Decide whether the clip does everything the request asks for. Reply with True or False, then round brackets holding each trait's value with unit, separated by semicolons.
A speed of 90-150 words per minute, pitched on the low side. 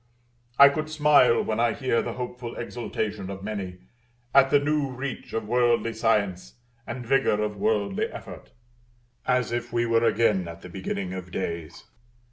False (160 wpm; 115 Hz)